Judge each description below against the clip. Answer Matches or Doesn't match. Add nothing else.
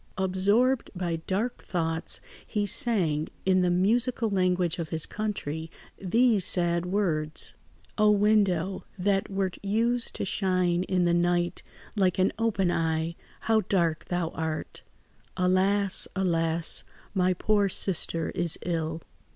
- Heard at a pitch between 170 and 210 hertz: Matches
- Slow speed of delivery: Matches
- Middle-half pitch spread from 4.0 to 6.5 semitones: Doesn't match